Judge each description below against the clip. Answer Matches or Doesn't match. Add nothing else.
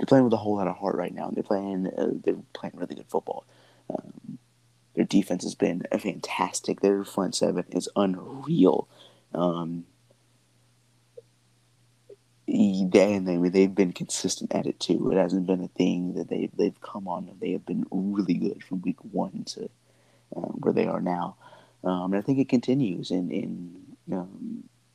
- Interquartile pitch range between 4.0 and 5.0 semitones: Matches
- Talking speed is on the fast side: Doesn't match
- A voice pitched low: Matches